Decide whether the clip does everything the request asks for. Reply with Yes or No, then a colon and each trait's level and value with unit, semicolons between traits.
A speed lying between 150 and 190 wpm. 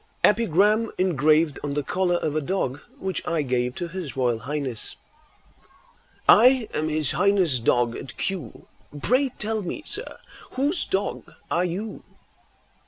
No: average, 140 wpm